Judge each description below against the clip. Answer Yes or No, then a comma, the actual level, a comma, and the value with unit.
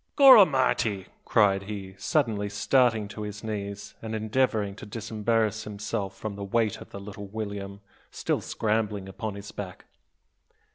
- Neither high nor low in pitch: No, low, 105 Hz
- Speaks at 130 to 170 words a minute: Yes, slow, 135 wpm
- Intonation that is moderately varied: No, narrow, 1.9 semitones